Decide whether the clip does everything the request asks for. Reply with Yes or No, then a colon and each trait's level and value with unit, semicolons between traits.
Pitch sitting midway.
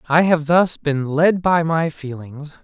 Yes: medium, 155 Hz